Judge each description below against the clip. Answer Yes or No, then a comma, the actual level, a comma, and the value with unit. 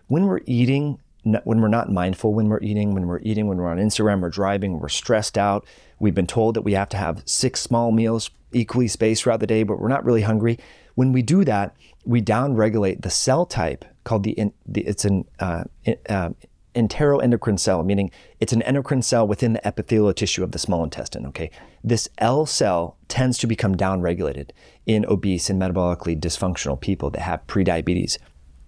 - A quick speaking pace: No, average, 185 wpm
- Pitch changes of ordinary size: Yes, average, 3.7 semitones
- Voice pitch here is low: Yes, low, 105 Hz